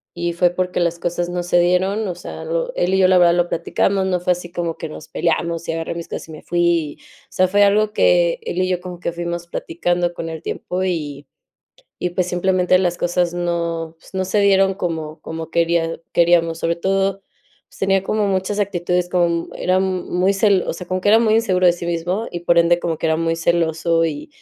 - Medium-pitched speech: Yes, medium, 175 Hz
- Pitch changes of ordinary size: No, narrow, 1.9 semitones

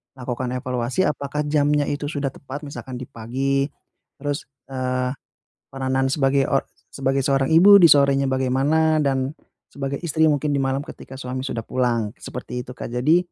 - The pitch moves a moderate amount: No, narrow, 2.1 semitones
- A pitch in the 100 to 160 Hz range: Yes, low, 135 Hz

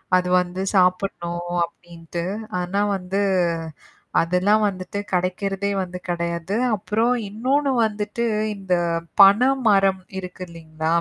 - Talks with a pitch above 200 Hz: No, medium, 185 Hz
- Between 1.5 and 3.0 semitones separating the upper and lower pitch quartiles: Yes, narrow, 2.5 semitones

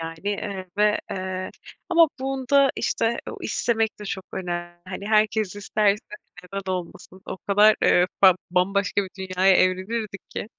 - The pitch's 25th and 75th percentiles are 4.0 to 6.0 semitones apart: No, narrow, 2.6 semitones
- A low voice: No, high, 195 Hz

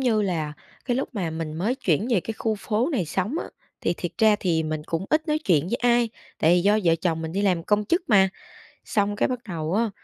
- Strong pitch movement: Yes, wide, 5.7 semitones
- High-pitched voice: Yes, high, 200 Hz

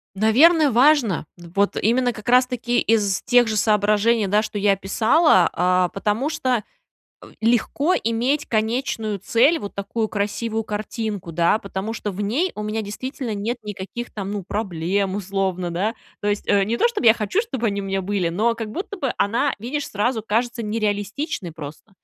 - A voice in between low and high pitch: No, high, 215 Hz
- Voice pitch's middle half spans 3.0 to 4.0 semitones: Yes, average, 3.3 semitones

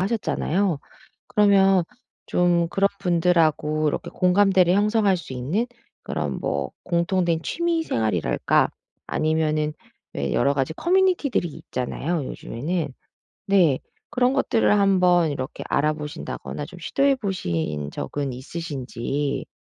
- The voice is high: No, medium, 170 Hz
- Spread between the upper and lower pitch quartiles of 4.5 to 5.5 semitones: Yes, average, 5.2 semitones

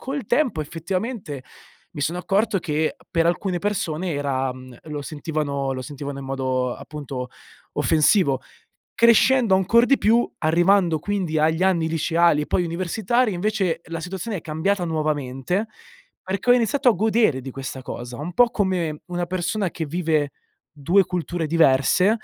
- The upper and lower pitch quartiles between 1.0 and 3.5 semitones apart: No, average, 5.1 semitones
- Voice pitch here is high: No, medium, 170 Hz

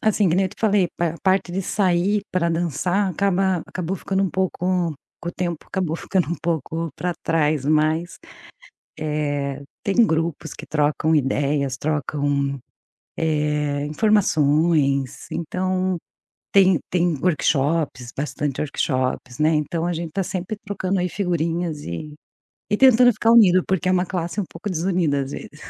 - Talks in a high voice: No, medium, 170 Hz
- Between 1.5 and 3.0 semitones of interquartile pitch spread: No, average, 3.8 semitones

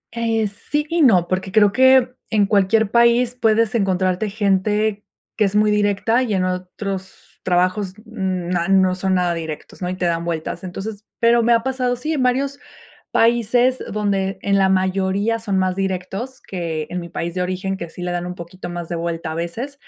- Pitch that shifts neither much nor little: Yes, average, 3.8 semitones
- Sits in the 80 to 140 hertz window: No, high, 195 Hz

